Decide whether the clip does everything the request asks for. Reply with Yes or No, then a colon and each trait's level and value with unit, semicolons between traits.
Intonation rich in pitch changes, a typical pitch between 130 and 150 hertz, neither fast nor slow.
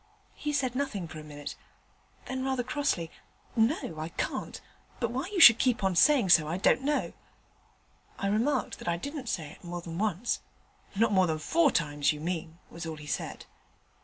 No: wide, 8.0 semitones; high, 195 Hz; average, 190 wpm